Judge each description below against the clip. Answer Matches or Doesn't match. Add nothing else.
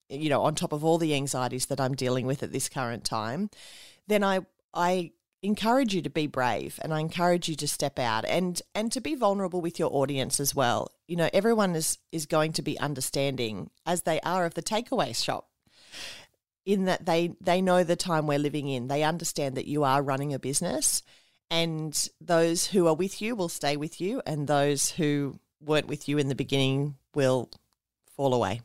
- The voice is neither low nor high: Matches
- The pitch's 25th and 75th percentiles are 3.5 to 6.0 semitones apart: Matches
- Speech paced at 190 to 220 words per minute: Matches